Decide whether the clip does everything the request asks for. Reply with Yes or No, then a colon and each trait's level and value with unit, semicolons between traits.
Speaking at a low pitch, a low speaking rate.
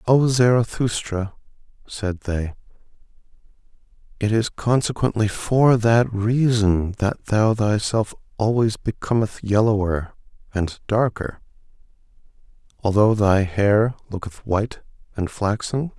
Yes: low, 110 Hz; slow, 95 wpm